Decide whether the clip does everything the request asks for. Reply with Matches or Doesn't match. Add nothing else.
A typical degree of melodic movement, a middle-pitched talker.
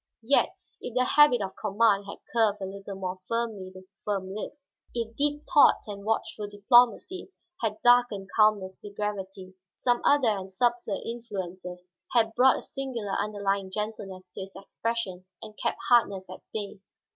Doesn't match